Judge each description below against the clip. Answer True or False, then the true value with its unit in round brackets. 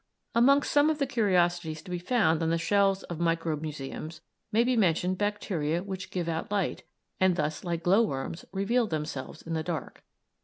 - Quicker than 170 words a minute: True (180 wpm)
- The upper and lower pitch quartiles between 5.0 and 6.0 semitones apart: False (4.2 semitones)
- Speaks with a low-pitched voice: False (175 Hz)